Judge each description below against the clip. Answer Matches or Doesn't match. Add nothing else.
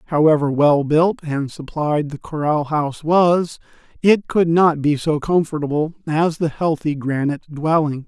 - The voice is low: Doesn't match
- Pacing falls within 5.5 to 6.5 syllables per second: Doesn't match